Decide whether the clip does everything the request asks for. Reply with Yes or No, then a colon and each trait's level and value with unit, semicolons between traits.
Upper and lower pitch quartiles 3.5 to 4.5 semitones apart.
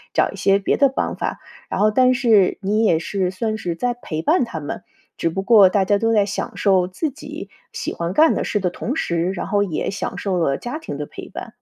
Yes: average, 4.2 semitones